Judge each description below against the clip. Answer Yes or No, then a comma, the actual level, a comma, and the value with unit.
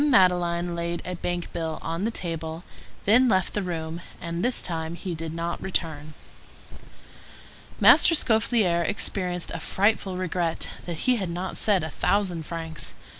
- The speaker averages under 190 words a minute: Yes, average, 150 wpm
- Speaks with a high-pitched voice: No, medium, 175 Hz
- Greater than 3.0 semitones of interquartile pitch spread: No, narrow, 2.5 semitones